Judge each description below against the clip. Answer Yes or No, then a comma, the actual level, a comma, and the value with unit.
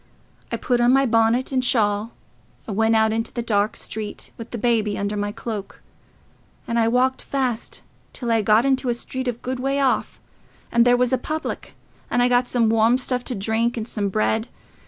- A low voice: No, high, 235 Hz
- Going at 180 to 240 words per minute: Yes, average, 200 wpm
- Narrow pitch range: Yes, narrow, 2.3 semitones